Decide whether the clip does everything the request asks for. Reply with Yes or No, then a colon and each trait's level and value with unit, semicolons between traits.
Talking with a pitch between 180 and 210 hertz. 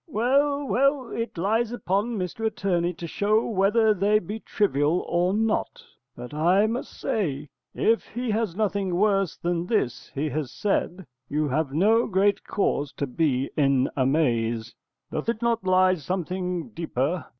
Yes: medium, 185 Hz